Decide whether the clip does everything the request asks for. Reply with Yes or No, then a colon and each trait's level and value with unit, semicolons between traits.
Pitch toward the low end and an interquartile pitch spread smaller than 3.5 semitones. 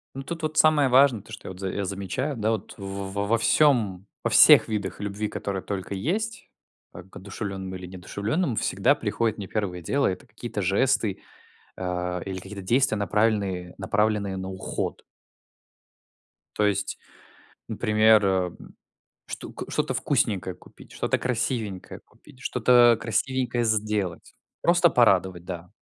No: low, 105 Hz; average, 3.8 semitones